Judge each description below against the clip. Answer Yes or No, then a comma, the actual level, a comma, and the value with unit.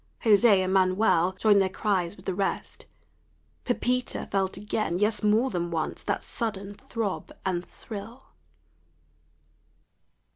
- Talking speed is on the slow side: Yes, slow, 120 wpm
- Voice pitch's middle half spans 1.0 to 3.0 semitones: Yes, average, 2.7 semitones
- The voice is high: Yes, high, 200 Hz